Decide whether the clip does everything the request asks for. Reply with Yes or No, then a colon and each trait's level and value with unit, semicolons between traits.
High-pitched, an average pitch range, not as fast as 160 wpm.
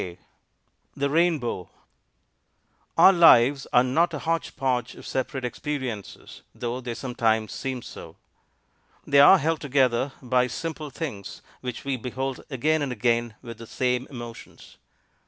No: low, 130 Hz; average, 3.3 semitones; average, 140 wpm